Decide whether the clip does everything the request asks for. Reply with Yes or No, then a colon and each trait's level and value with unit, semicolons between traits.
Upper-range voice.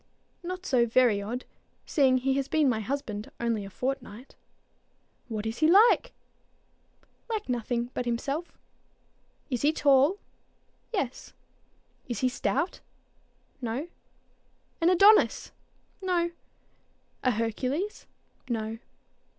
Yes: very high, 255 Hz